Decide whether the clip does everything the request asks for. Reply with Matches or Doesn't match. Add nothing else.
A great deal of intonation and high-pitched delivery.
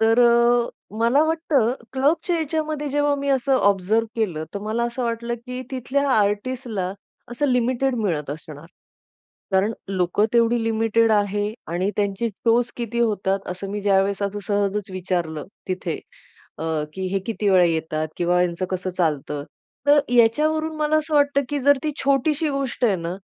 Matches